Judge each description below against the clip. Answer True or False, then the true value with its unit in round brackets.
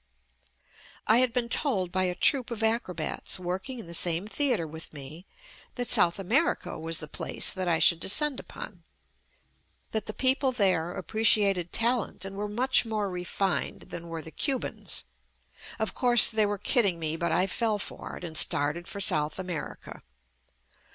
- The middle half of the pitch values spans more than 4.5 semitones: True (5.1 semitones)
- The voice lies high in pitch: True (195 Hz)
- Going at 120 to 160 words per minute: False (180 wpm)